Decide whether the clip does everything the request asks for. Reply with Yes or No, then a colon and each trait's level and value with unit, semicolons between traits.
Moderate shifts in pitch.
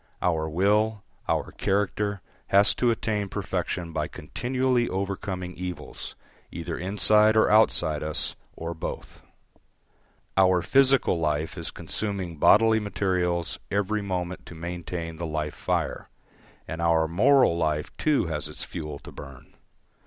Yes: average, 4.2 semitones